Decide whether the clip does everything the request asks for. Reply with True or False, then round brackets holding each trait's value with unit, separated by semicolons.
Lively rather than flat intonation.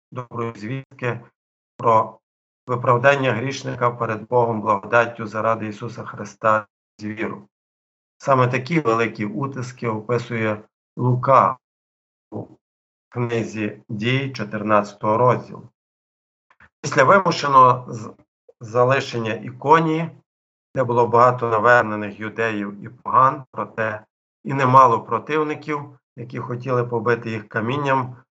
False (2.8 semitones)